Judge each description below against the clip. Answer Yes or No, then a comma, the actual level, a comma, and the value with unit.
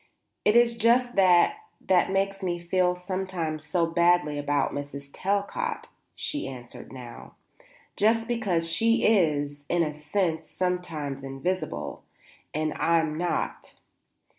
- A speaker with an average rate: No, slow, 120 wpm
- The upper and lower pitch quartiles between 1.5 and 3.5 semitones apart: No, average, 4.6 semitones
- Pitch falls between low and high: Yes, medium, 175 Hz